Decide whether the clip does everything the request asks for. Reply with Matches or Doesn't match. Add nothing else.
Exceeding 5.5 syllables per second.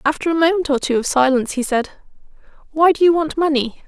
Matches